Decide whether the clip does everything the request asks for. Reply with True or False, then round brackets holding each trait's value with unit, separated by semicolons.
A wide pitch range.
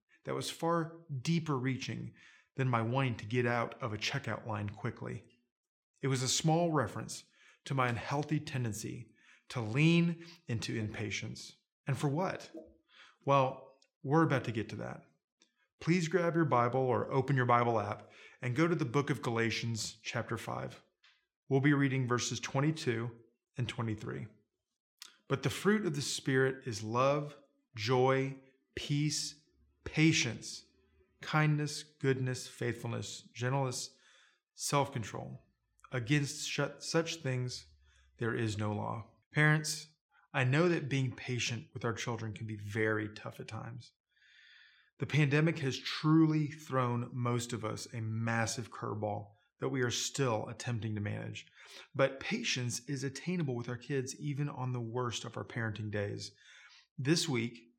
False (4.0 semitones)